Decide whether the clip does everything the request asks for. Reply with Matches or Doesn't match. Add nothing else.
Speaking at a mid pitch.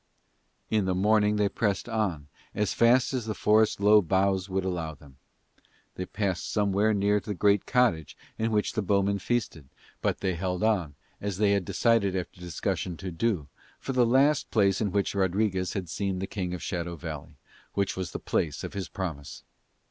Doesn't match